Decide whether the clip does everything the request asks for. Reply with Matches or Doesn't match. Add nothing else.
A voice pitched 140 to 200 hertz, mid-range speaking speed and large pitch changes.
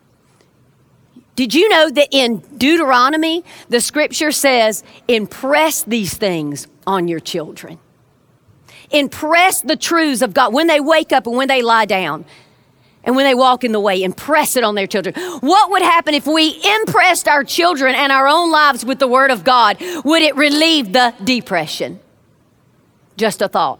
Doesn't match